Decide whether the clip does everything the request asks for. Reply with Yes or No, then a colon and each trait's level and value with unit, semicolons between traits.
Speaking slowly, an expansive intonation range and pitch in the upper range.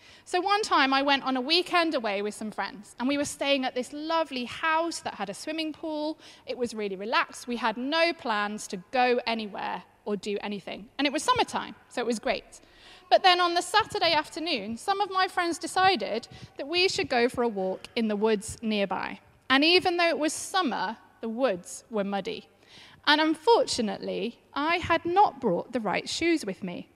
No: average, 200 wpm; wide, 7.3 semitones; very high, 285 Hz